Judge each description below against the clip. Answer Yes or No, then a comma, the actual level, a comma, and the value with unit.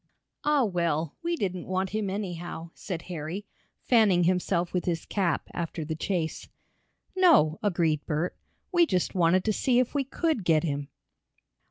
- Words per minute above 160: No, average, 155 wpm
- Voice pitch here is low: No, medium, 180 Hz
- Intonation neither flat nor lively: Yes, average, 4.2 semitones